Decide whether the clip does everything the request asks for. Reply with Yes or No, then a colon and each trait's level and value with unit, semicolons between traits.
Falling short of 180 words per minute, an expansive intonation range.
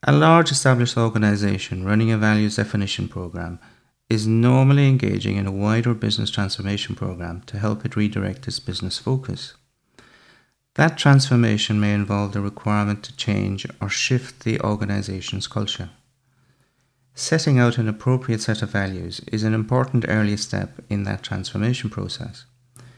No: average, 140 wpm; average, 3.5 semitones